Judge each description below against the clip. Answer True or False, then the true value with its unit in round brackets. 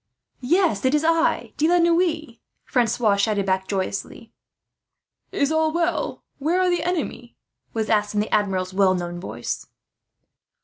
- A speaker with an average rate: True (145 wpm)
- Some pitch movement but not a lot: False (8.5 semitones)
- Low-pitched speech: False (240 Hz)